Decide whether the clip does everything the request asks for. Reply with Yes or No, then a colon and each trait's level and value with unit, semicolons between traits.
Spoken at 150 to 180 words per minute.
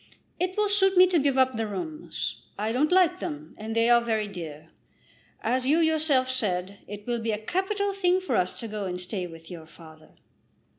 No: fast, 205 wpm